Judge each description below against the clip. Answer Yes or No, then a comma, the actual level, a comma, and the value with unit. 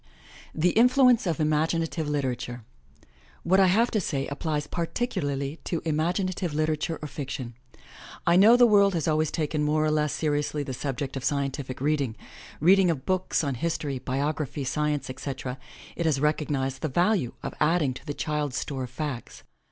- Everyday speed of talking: Yes, average, 170 wpm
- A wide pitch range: No, average, 3.5 semitones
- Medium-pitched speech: Yes, medium, 150 Hz